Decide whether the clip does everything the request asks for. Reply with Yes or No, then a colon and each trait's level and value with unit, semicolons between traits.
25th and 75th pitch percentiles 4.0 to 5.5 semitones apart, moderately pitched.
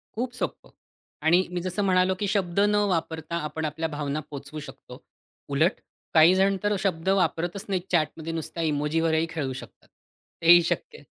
No: average, 2.9 semitones; medium, 165 Hz